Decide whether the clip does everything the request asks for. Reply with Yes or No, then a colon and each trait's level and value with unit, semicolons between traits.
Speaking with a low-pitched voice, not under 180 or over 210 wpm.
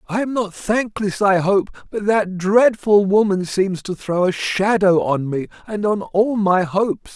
No: high, 195 Hz; average, 185 wpm